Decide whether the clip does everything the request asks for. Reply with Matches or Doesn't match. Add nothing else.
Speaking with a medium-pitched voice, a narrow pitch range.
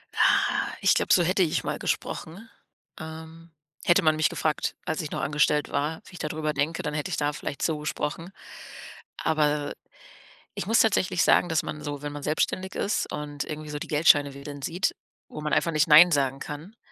Matches